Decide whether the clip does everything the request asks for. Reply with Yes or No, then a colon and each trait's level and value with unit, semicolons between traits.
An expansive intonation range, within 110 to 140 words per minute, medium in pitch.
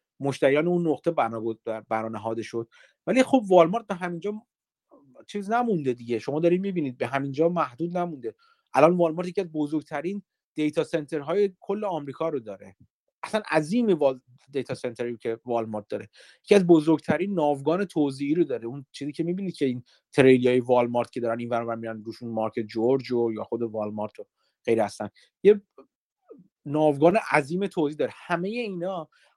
No: wide, 6.9 semitones; fast, 155 wpm; medium, 150 Hz